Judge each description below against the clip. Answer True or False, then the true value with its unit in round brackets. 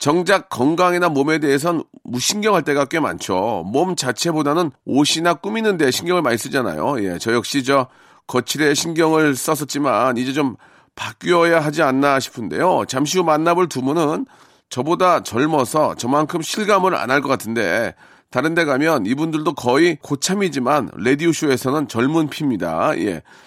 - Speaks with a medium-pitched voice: True (150 Hz)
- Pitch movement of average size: True (4.2 semitones)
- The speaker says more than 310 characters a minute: True (330 characters per minute)